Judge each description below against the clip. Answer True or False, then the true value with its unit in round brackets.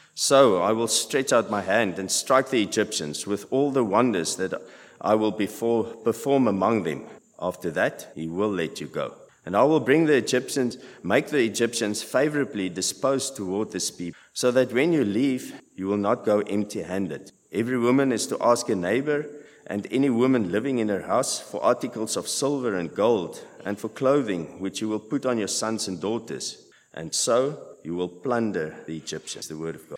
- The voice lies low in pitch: True (110 Hz)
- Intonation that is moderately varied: True (4.9 semitones)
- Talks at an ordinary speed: True (190 wpm)